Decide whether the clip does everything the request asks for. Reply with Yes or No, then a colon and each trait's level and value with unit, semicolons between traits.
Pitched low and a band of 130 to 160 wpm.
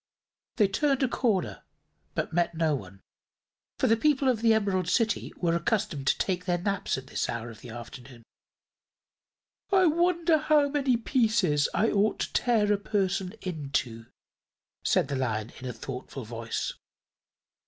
No: medium, 185 Hz; average, 155 wpm